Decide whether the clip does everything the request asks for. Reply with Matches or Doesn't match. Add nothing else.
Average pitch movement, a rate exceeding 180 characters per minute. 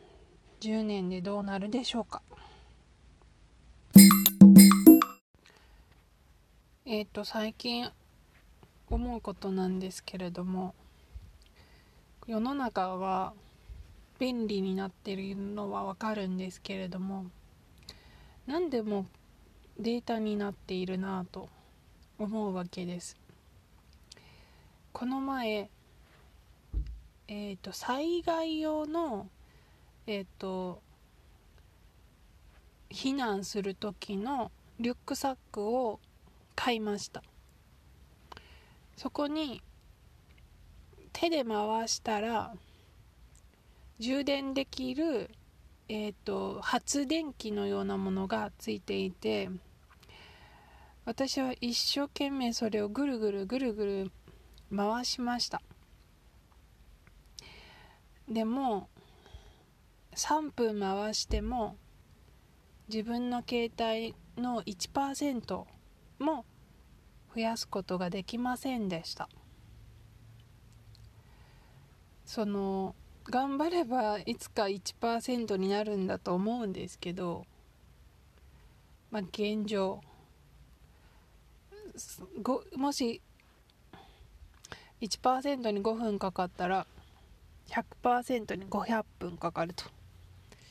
Doesn't match